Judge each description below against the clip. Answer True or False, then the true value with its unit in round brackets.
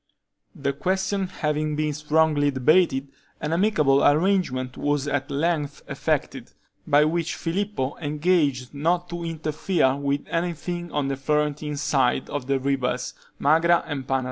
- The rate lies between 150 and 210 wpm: False (135 wpm)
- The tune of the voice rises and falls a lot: False (3.2 semitones)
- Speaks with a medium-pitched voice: True (150 Hz)